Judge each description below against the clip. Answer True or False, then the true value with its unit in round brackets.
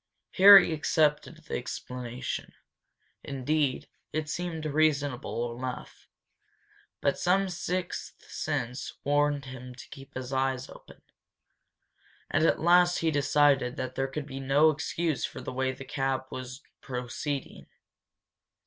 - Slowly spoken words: True (120 wpm)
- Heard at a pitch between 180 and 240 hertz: False (140 Hz)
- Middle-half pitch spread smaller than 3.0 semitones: False (3.3 semitones)